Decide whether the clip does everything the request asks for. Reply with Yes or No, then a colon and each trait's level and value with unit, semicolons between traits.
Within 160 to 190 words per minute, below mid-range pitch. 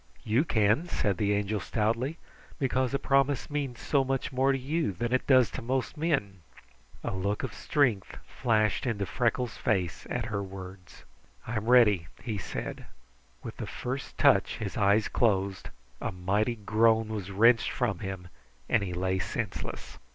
Yes: average, 165 wpm; low, 110 Hz